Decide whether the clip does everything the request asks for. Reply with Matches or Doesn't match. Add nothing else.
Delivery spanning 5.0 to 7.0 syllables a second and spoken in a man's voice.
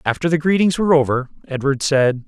Matches